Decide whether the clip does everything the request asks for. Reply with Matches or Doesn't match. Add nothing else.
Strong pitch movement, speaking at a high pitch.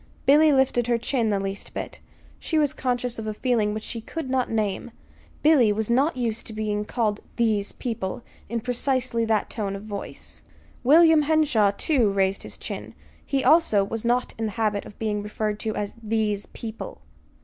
Doesn't match